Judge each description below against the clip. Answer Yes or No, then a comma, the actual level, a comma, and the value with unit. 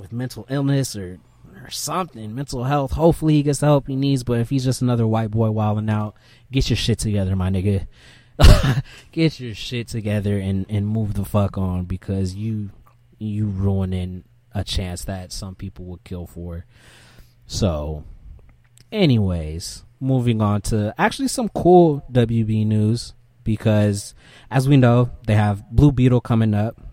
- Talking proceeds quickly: No, average, 160 wpm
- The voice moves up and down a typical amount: Yes, average, 4.1 semitones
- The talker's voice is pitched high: No, low, 110 Hz